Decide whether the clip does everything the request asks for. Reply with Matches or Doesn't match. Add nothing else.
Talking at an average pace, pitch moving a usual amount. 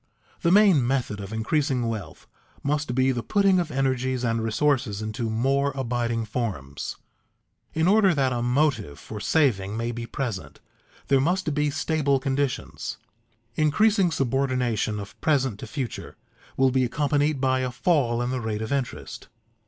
Matches